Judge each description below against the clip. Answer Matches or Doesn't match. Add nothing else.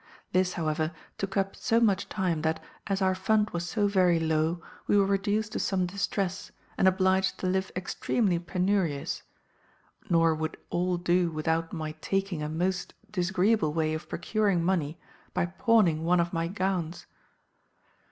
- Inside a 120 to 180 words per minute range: Matches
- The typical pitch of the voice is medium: Matches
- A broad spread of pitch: Doesn't match